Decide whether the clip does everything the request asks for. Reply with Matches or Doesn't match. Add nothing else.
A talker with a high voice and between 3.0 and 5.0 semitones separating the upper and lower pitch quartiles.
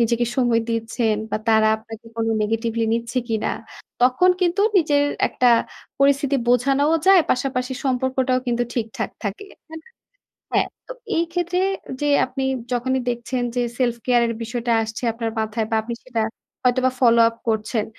Doesn't match